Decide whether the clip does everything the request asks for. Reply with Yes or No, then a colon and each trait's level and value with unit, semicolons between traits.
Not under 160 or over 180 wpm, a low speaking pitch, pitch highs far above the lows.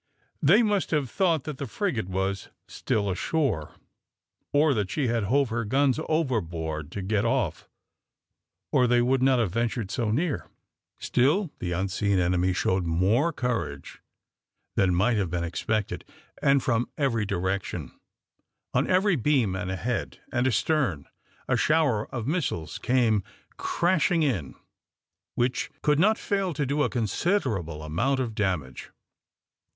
No: average, 140 wpm; low, 120 Hz; wide, 7.0 semitones